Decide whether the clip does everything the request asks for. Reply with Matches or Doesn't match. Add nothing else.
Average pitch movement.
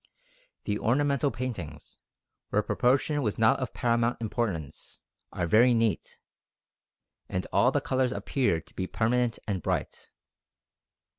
Matches